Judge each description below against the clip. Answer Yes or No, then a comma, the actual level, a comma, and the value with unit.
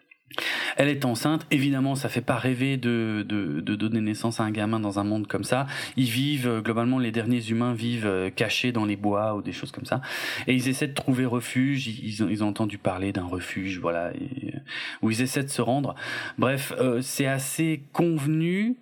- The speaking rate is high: No, average, 205 wpm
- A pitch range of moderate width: Yes, average, 4.1 semitones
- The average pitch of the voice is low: Yes, low, 120 Hz